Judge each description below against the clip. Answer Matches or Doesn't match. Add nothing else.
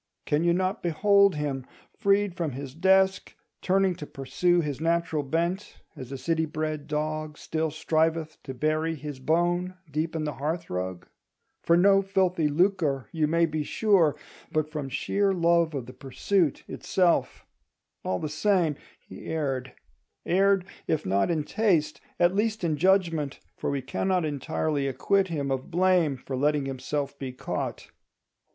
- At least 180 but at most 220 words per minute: Doesn't match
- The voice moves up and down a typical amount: Matches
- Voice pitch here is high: Doesn't match